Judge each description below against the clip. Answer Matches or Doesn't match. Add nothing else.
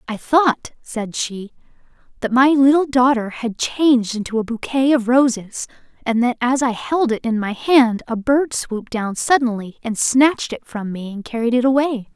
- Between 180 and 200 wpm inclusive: Matches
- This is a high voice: Matches